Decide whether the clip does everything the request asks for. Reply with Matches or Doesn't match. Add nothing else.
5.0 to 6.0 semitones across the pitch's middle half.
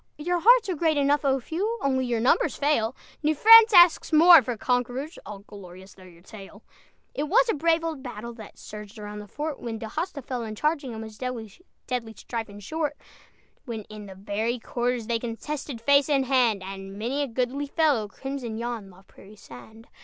Matches